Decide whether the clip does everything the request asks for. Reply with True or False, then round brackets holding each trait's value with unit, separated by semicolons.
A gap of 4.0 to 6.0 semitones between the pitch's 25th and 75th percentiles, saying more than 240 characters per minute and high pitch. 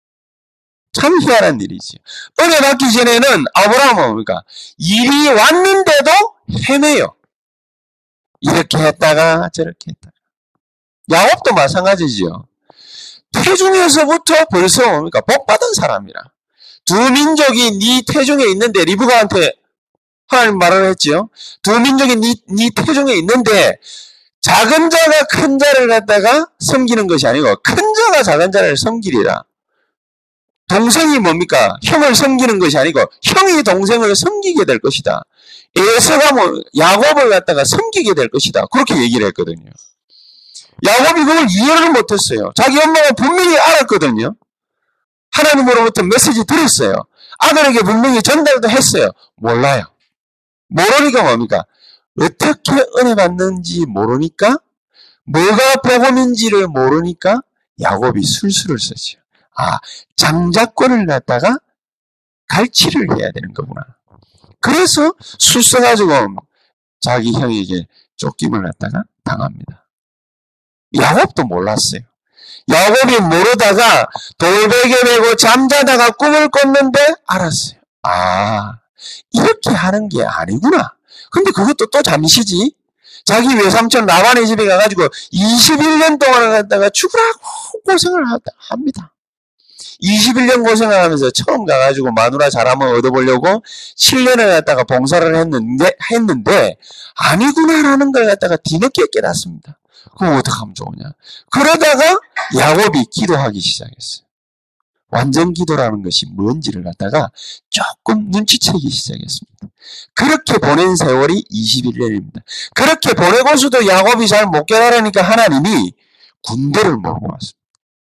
False (8.9 semitones; 285 characters per minute; 240 Hz)